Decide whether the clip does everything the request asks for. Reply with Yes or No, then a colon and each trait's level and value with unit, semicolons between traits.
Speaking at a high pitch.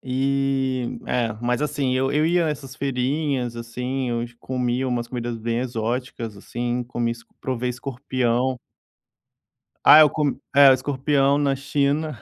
No: low, 130 Hz